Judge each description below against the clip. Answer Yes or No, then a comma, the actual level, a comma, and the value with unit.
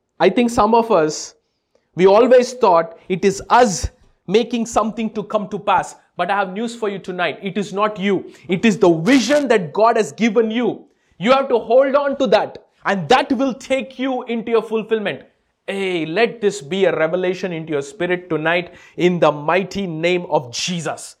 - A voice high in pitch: Yes, high, 205 Hz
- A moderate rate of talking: Yes, average, 190 wpm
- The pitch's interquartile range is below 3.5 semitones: No, average, 4.7 semitones